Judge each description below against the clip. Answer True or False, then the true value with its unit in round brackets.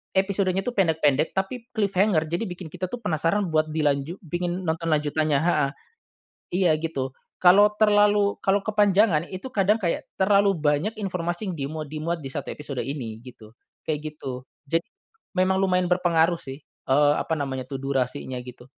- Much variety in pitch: False (4.7 semitones)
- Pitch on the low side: False (165 Hz)